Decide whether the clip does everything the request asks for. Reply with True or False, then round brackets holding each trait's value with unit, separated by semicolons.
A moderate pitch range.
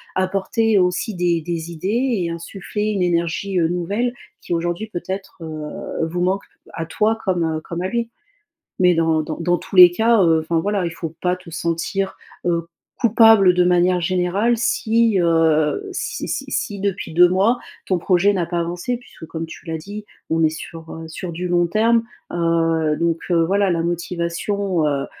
True (3.2 semitones)